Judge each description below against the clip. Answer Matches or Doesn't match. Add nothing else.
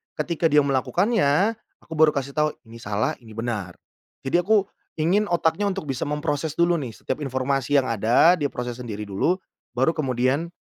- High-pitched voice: Doesn't match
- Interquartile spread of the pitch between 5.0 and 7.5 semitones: Matches